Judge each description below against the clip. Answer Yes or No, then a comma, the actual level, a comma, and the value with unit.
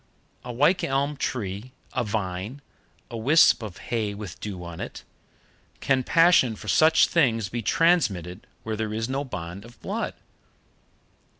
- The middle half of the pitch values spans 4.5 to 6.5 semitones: Yes, average, 5.1 semitones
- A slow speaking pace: No, average, 145 wpm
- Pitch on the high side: No, low, 115 Hz